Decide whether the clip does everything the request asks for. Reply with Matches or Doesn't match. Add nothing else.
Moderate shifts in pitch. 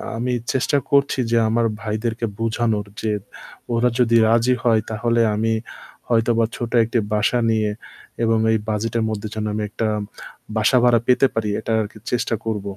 Doesn't match